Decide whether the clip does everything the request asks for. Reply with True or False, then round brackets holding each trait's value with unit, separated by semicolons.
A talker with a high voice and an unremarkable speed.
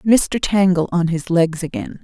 False (175 Hz; 175 wpm)